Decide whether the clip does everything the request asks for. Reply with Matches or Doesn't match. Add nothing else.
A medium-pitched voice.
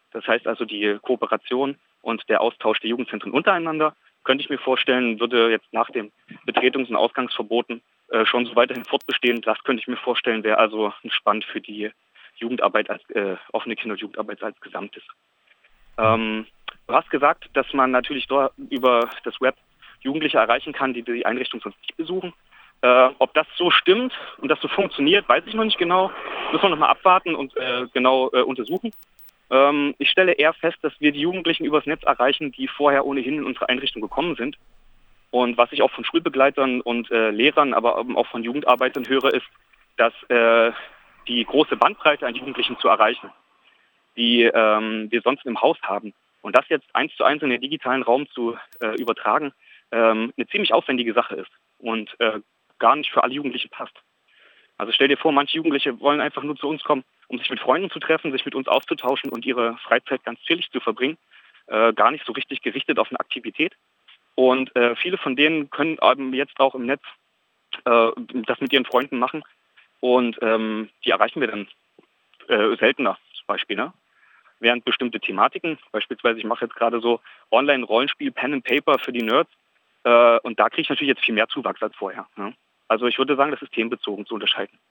Doesn't match